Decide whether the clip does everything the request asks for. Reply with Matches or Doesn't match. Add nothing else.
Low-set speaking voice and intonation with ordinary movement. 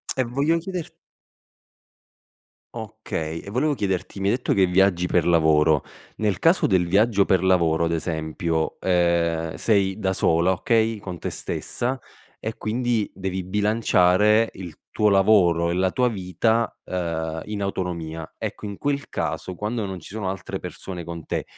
Matches